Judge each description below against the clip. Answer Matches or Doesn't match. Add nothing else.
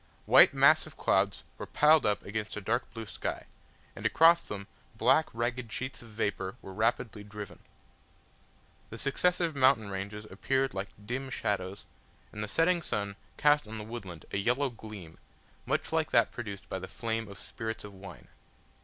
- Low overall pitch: Matches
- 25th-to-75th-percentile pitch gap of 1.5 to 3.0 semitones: Doesn't match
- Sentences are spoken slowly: Doesn't match